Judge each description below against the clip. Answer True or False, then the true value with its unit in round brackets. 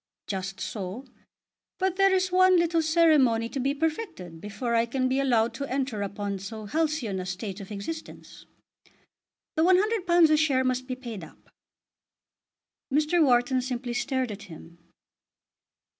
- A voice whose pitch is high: True (255 Hz)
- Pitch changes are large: True (7.2 semitones)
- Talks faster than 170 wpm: False (145 wpm)